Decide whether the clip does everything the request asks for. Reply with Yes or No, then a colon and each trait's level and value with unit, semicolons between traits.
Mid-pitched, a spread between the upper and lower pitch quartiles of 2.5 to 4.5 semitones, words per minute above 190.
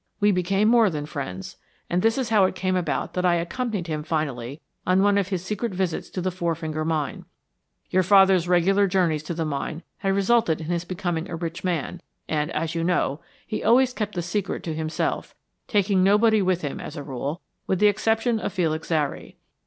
Yes: medium, 180 Hz; average, 3.8 semitones; fast, 205 wpm